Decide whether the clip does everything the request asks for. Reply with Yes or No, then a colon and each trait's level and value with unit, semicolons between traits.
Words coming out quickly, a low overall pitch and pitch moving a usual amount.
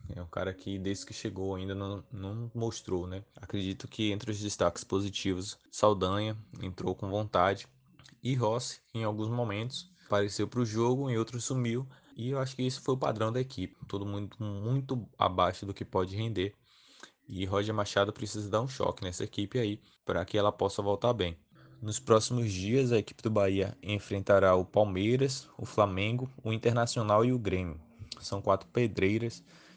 No: average, 175 wpm; low, 105 Hz; average, 3.5 semitones